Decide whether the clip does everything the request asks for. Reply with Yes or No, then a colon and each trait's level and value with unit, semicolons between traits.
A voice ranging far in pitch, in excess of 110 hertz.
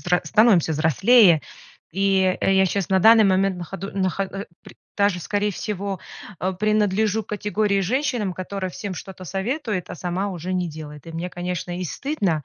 No: narrow, 2.6 semitones; high, 190 Hz